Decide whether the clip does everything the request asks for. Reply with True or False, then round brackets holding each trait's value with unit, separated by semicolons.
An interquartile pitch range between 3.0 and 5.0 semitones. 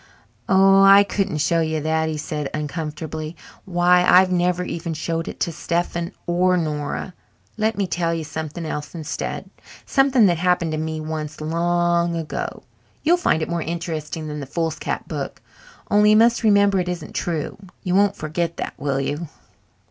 False (2.6 semitones)